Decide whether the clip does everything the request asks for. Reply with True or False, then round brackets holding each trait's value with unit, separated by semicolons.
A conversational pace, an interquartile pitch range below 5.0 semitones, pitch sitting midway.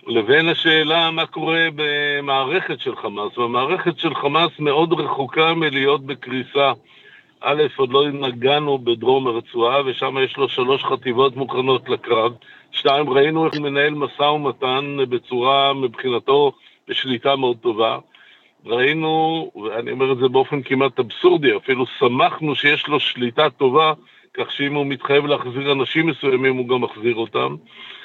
True (135 wpm; 3.4 semitones; 145 Hz)